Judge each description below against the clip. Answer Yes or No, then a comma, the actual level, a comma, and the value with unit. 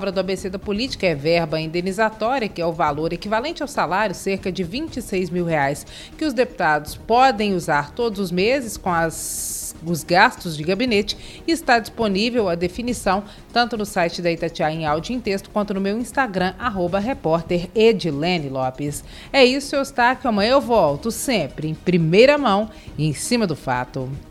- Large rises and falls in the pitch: Yes, wide, 6.0 semitones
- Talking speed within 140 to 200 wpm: Yes, average, 180 wpm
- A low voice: No, high, 195 Hz